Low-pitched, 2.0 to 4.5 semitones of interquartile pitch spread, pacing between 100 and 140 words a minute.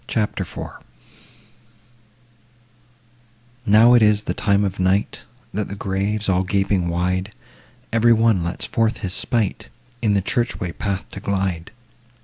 Yes: low, 100 Hz; narrow, 2.5 semitones; slow, 135 wpm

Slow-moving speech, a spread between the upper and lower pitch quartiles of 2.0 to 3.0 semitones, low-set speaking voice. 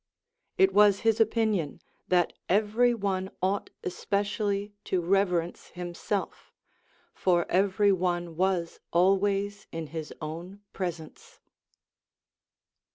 No: slow, 105 wpm; narrow, 2.6 semitones; high, 190 Hz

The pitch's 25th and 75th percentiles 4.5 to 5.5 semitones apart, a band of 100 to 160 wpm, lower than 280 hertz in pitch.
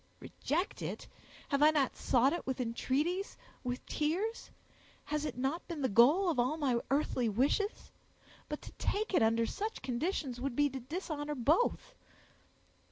No: average, 5.1 semitones; average, 155 wpm; very high, 290 Hz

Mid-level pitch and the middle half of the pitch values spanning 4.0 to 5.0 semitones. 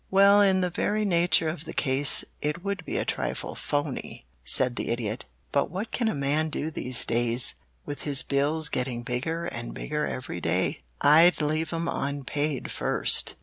Yes: medium, 150 Hz; average, 4.5 semitones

